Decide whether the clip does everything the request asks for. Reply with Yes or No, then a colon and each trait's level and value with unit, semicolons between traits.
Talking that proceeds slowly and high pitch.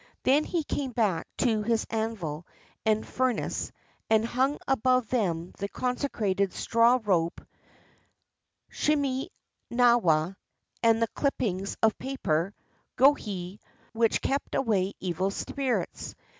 Yes: slow, 115 wpm; high, 225 Hz